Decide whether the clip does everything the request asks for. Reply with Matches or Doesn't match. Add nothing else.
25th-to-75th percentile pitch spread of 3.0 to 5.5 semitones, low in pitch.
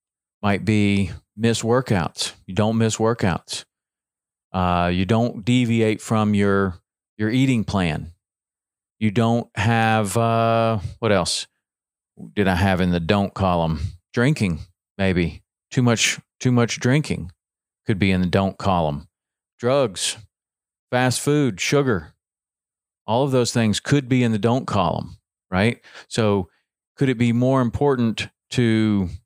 Matches